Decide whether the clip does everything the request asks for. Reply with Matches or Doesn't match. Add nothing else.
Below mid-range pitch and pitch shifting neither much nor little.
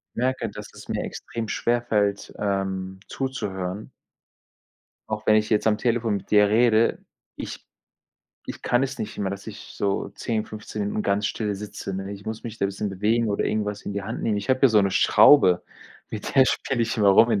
Doesn't match